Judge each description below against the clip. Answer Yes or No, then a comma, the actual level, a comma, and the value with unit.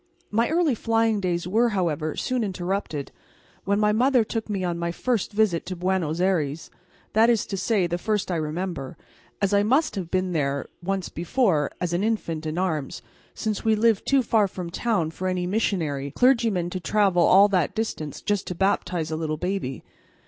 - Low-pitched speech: No, medium, 185 Hz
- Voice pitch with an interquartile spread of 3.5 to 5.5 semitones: Yes, average, 4.3 semitones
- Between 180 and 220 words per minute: Yes, average, 190 wpm